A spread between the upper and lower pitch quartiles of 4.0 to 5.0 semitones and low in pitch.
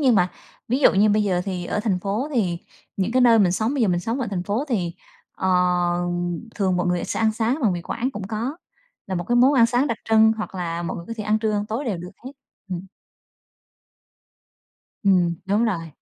No: average, 4.3 semitones; high, 210 Hz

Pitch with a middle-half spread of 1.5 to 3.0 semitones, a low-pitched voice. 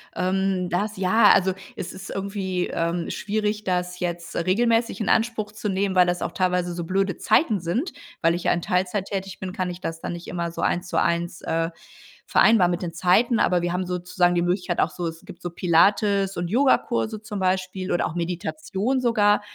No: average, 2.7 semitones; medium, 185 Hz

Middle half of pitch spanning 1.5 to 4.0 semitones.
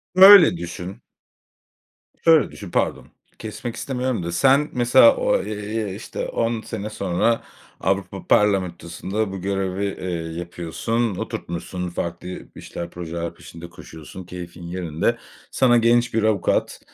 No: average, 4.8 semitones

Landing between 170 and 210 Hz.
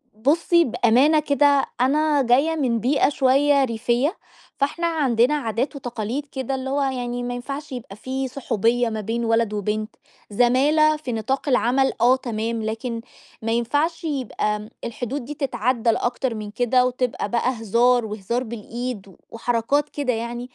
No: high, 245 Hz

